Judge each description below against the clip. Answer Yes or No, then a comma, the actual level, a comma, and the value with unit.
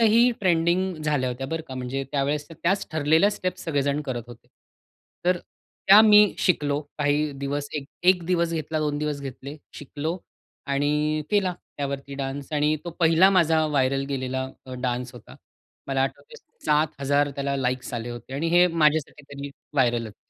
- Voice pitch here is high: No, medium, 145 Hz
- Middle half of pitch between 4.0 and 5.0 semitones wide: No, average, 3.3 semitones